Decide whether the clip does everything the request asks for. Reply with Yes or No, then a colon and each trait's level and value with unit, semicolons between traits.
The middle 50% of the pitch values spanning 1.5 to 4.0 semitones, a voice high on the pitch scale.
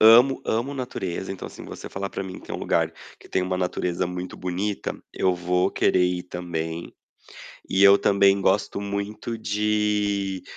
No: narrow, 2.4 semitones; very low, 95 Hz